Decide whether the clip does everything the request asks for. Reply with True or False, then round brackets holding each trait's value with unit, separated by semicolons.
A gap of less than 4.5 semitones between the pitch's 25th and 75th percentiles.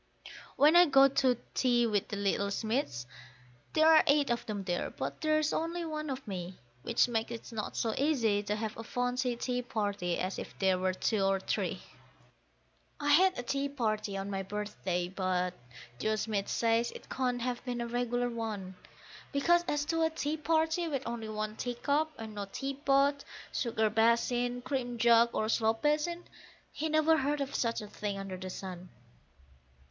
False (5.3 semitones)